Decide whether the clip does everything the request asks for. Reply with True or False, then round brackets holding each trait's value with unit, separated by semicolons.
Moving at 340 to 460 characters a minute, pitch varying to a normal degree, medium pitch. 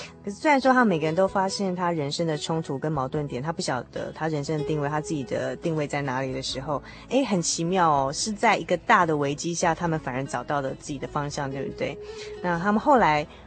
True (350 characters per minute; 4.5 semitones; 155 Hz)